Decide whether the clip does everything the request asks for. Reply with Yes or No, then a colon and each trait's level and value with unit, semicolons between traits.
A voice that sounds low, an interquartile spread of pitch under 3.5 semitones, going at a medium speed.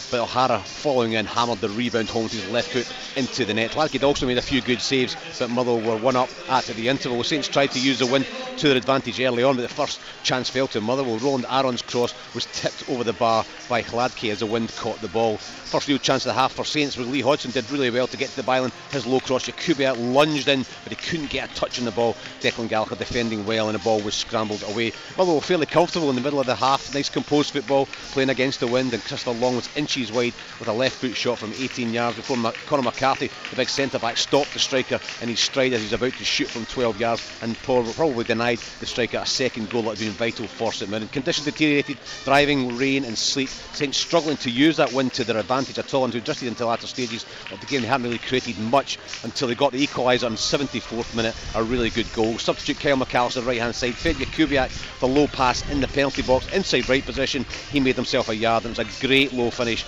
No: low, 125 Hz; average, 2.9 semitones; fast, 245 wpm